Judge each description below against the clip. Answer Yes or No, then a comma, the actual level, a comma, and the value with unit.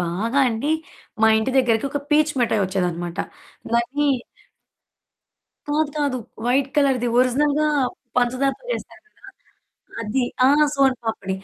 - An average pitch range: Yes, average, 4.1 semitones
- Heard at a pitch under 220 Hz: No, very high, 255 Hz